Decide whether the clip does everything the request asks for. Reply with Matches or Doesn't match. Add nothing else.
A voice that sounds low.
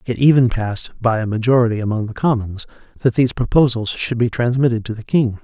Matches